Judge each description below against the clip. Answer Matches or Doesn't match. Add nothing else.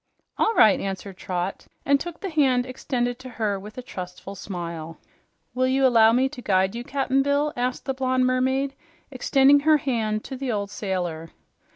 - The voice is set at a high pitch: Matches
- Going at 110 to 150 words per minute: Doesn't match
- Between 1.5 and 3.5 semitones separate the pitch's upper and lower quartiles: Doesn't match